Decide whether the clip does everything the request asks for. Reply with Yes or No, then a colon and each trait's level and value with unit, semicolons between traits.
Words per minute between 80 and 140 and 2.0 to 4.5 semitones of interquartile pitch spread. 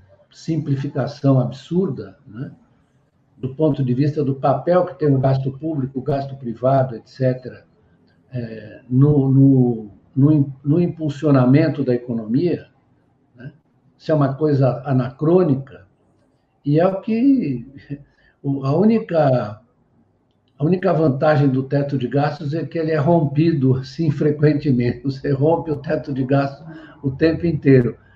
Yes: average, 130 wpm; average, 3.0 semitones